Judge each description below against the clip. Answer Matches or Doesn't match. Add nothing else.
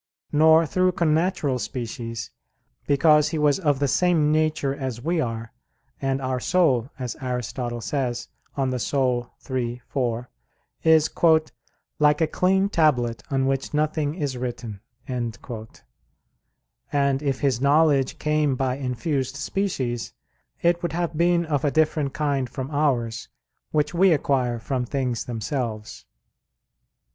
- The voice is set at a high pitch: Doesn't match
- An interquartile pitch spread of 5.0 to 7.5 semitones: Doesn't match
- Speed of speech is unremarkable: Doesn't match